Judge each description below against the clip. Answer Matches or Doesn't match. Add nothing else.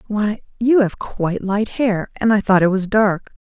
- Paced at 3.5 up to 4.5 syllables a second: Matches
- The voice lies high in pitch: Matches